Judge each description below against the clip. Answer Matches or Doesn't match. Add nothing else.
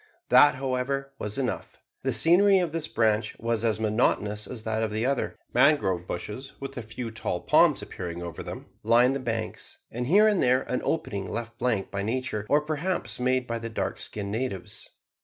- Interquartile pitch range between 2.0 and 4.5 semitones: Matches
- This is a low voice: Matches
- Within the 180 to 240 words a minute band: Matches